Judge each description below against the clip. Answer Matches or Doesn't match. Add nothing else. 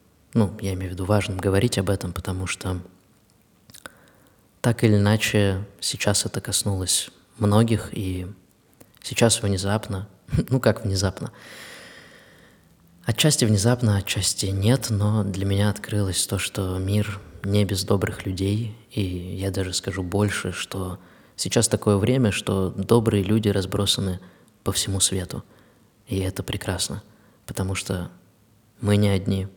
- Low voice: Matches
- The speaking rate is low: Doesn't match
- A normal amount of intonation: Doesn't match